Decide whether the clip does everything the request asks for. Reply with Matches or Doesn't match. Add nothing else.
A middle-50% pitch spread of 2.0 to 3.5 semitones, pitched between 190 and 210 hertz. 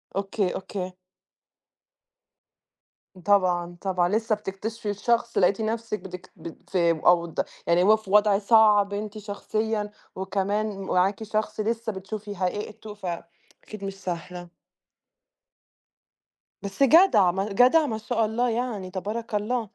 Matches